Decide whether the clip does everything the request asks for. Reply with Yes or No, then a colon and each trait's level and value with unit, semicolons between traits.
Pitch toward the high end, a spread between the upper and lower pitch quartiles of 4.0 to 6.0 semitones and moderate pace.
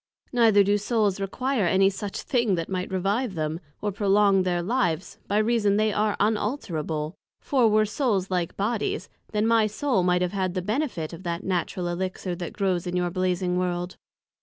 No: high, 195 Hz; average, 3.1 semitones; average, 180 wpm